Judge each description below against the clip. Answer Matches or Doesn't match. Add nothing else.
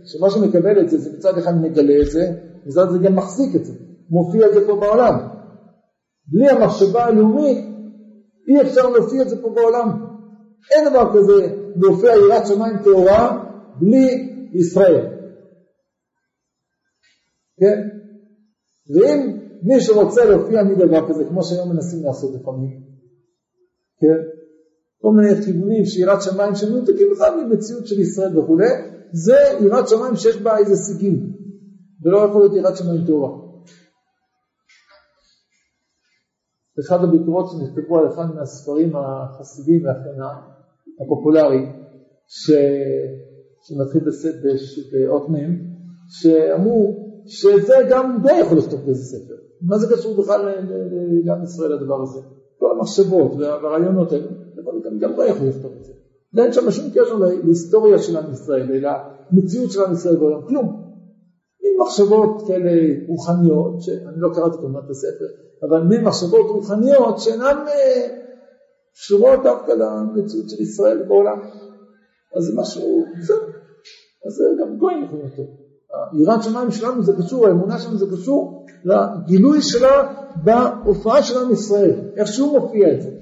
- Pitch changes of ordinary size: Doesn't match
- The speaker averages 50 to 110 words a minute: Doesn't match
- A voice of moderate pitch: Doesn't match